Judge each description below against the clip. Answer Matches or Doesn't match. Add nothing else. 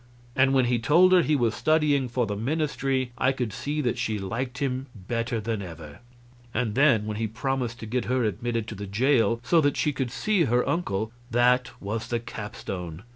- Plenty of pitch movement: Doesn't match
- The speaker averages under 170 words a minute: Doesn't match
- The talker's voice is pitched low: Matches